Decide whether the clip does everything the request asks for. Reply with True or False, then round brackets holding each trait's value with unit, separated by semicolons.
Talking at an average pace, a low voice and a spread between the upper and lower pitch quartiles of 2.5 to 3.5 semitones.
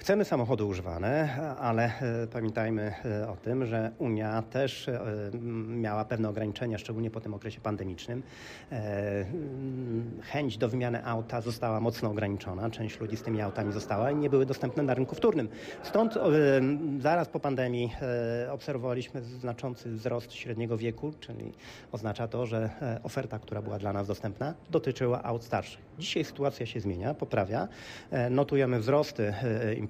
True (135 wpm; 120 Hz; 3.2 semitones)